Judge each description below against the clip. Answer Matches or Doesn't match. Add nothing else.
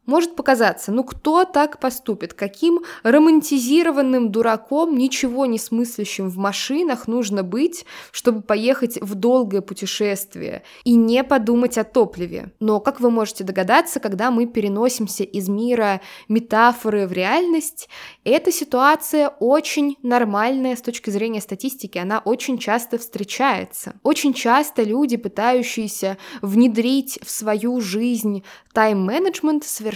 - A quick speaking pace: Doesn't match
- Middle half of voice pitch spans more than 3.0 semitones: Matches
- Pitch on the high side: Matches